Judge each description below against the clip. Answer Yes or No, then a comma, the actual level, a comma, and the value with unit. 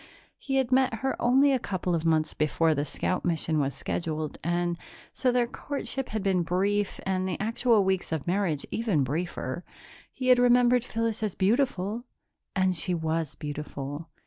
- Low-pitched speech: No, medium, 185 Hz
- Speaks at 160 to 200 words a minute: Yes, average, 170 wpm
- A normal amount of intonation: No, wide, 6.7 semitones